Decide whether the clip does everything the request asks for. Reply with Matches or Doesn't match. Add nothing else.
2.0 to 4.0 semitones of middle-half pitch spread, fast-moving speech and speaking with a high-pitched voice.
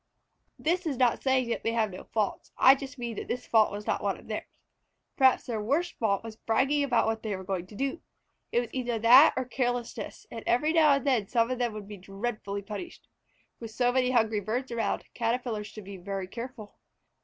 Matches